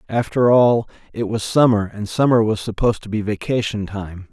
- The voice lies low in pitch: Yes, low, 110 Hz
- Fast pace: No, average, 165 wpm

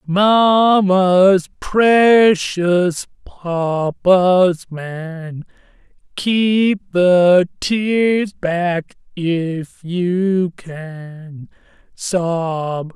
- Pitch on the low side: No, medium, 180 Hz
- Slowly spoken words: Yes, slow, 50 wpm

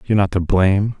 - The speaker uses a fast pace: Yes, fast, 240 wpm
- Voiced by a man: Yes, male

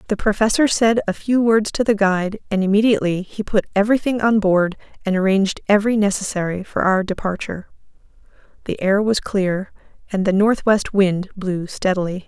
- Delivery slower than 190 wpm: Yes, average, 155 wpm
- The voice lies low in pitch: No, high, 200 Hz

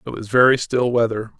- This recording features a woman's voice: No, male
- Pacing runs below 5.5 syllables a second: No, 5.8 syllables/s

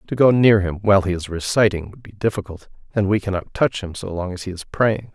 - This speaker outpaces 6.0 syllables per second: No, 5.9 syllables/s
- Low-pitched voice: Yes, low, 100 Hz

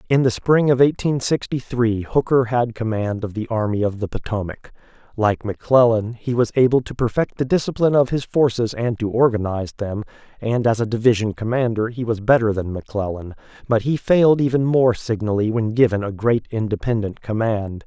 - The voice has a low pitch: Yes, low, 115 Hz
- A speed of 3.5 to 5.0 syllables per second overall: No, 5.5 syllables/s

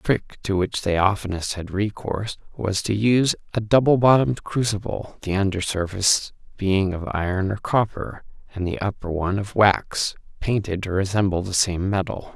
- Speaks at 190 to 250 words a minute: No, average, 170 wpm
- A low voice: Yes, low, 100 Hz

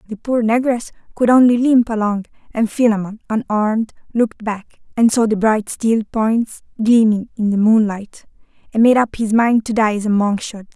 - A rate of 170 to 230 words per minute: Yes, average, 185 wpm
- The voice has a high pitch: Yes, high, 220 Hz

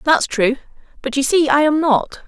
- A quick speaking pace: Yes, fast, 210 wpm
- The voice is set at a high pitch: Yes, very high, 285 Hz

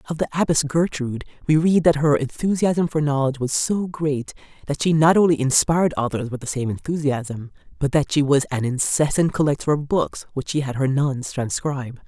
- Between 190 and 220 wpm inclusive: Yes, average, 195 wpm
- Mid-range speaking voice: Yes, medium, 145 Hz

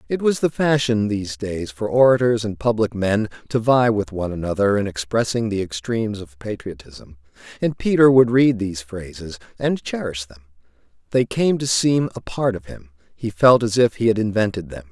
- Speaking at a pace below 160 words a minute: No, average, 190 wpm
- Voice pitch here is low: Yes, low, 110 Hz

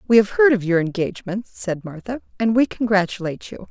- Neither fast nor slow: Yes, average, 195 wpm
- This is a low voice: No, high, 205 Hz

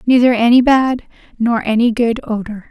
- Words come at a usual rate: Yes, average, 155 wpm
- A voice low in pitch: No, high, 235 Hz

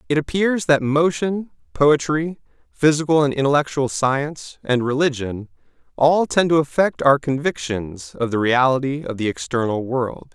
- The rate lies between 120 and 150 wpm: Yes, average, 140 wpm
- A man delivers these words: Yes, male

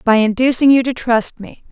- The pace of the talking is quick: Yes, fast, 210 wpm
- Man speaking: No, female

